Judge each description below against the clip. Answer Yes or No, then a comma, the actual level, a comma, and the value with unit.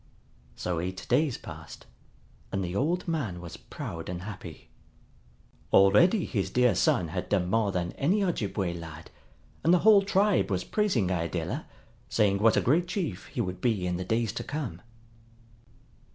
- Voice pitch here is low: Yes, low, 100 Hz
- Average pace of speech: Yes, average, 160 wpm